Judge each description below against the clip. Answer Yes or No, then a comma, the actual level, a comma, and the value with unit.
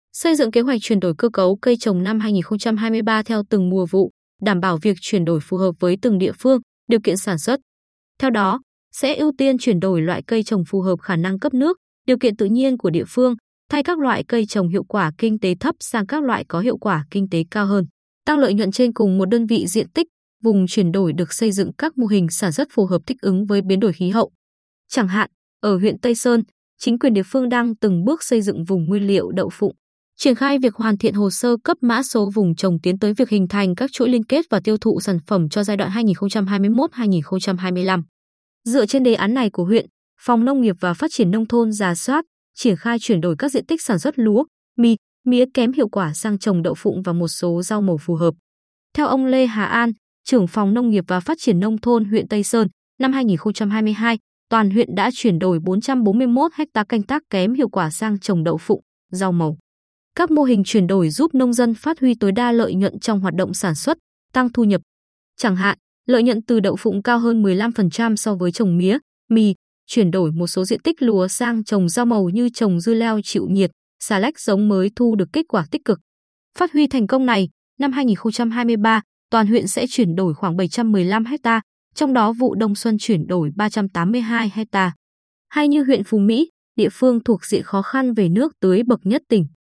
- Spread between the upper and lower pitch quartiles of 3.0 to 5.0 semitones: Yes, average, 4.2 semitones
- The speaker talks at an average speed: Yes, average, 225 wpm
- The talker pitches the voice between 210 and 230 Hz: Yes, high, 215 Hz